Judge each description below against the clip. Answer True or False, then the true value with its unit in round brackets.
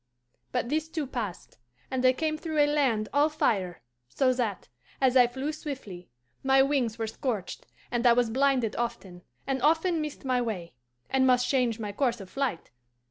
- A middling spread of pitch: True (3.9 semitones)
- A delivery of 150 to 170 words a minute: False (180 wpm)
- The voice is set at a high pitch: True (255 Hz)